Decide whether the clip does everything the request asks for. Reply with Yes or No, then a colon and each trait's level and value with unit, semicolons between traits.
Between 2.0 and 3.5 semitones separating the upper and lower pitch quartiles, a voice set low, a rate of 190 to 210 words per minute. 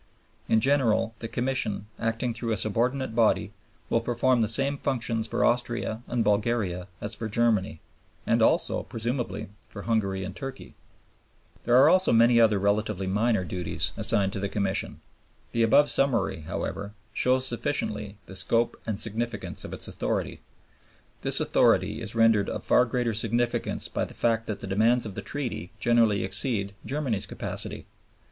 No: average, 2.9 semitones; low, 115 Hz; average, 155 wpm